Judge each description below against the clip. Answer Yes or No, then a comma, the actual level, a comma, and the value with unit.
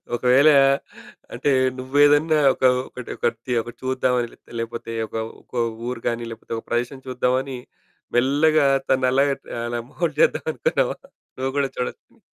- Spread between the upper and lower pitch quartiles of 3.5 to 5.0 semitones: No, average, 2.8 semitones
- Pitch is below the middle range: Yes, low, 130 Hz